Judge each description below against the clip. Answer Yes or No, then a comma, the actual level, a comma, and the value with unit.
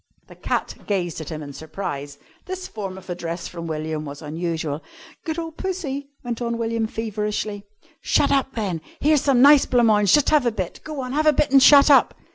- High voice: Yes, high, 220 Hz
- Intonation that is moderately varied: No, wide, 8.7 semitones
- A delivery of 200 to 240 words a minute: Yes, fast, 205 wpm